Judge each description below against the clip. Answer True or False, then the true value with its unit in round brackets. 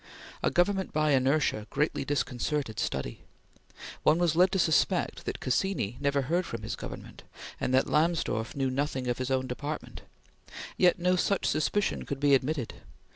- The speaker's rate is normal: True (160 wpm)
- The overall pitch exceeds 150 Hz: False (145 Hz)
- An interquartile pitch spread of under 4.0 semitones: False (4.7 semitones)